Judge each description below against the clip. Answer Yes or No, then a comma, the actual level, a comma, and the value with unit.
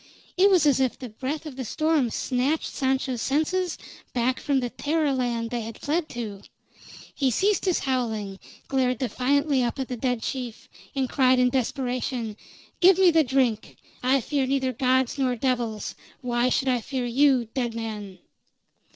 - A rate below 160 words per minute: No, average, 170 wpm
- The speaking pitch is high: Yes, very high, 255 Hz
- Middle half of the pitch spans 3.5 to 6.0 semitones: No, average, 2.7 semitones